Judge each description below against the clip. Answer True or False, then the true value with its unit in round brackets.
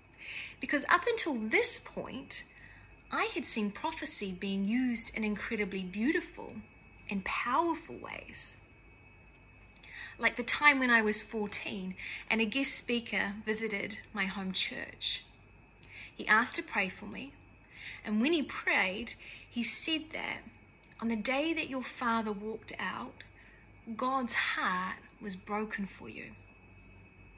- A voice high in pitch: True (225 Hz)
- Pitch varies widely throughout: True (5.7 semitones)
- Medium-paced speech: False (130 wpm)